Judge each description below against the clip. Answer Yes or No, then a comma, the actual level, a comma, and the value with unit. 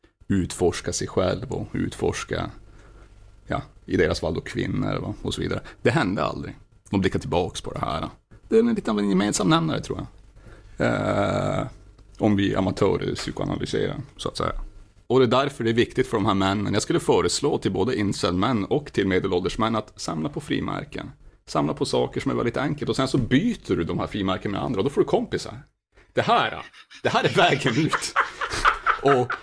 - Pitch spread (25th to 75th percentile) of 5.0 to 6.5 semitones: No, average, 4.0 semitones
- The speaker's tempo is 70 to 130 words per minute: No, average, 190 wpm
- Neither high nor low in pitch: No, low, 105 Hz